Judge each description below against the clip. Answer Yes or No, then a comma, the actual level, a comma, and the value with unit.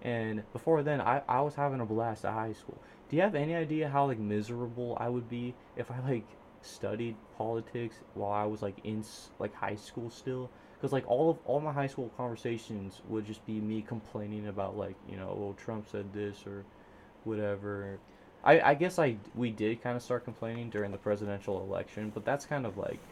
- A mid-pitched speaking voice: No, low, 110 Hz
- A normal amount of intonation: Yes, average, 3.0 semitones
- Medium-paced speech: No, fast, 210 wpm